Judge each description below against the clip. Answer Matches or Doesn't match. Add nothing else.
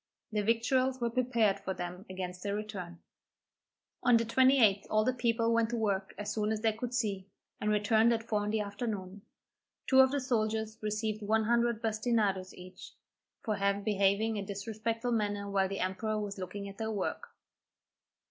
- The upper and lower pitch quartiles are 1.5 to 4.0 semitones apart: Matches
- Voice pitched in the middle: Doesn't match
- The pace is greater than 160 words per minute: Matches